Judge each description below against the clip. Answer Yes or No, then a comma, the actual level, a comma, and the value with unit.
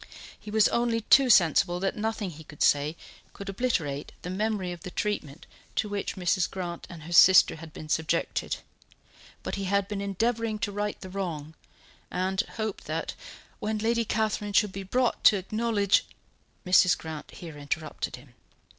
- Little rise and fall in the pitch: No, average, 4.0 semitones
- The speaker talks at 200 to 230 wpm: No, average, 170 wpm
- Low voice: No, high, 195 Hz